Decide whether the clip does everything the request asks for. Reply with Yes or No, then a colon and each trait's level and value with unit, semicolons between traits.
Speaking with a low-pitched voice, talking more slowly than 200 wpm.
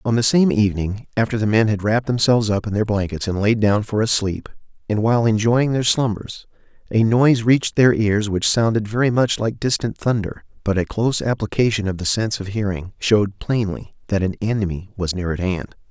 No: low, 105 Hz; fast, 205 wpm